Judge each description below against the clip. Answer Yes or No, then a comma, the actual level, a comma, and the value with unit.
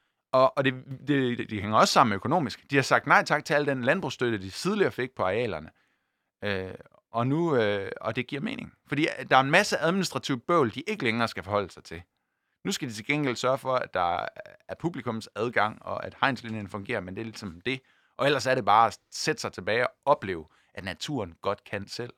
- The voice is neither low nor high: No, low, 125 Hz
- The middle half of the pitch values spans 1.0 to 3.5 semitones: No, average, 4.8 semitones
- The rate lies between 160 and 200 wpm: No, average, 220 wpm